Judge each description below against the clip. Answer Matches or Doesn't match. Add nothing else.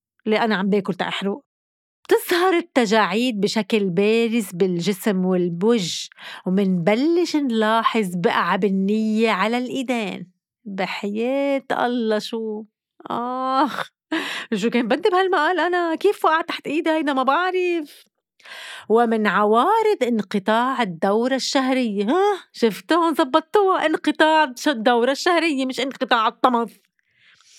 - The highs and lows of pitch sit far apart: Matches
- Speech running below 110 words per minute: Matches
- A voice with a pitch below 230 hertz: Doesn't match